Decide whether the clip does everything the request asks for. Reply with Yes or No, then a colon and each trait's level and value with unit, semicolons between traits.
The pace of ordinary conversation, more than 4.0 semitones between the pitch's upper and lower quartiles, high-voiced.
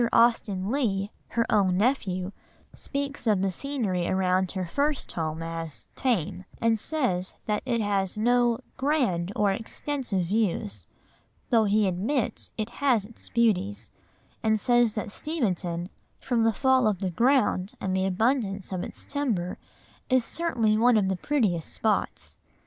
Yes: average, 145 wpm; average, 4.7 semitones; high, 215 Hz